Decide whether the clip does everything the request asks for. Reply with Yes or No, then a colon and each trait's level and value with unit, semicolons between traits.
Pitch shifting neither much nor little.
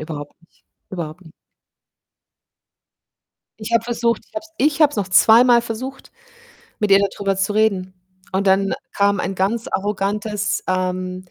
Yes: average, 3.4 semitones